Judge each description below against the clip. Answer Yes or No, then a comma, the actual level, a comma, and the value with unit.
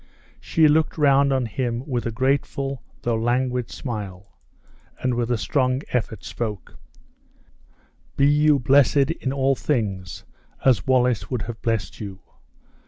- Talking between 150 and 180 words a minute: No, slow, 135 wpm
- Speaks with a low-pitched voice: Yes, low, 125 Hz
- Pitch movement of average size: Yes, average, 3.3 semitones